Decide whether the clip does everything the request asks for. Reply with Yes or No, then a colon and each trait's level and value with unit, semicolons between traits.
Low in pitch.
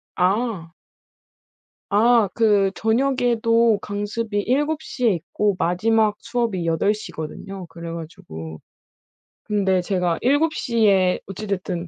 No: high, 205 Hz